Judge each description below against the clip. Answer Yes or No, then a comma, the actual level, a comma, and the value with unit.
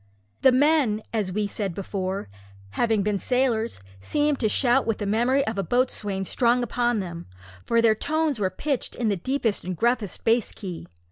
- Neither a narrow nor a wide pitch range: Yes, average, 4.0 semitones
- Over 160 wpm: Yes, average, 180 wpm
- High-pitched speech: Yes, high, 225 Hz